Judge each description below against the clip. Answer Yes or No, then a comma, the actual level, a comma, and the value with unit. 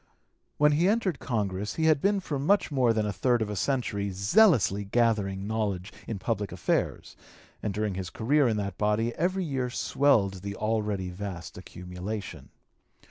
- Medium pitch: No, low, 110 Hz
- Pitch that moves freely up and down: Yes, wide, 5.7 semitones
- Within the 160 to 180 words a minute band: Yes, average, 165 wpm